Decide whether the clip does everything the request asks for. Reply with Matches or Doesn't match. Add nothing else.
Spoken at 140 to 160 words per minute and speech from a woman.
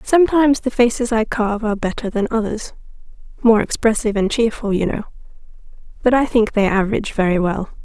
Matches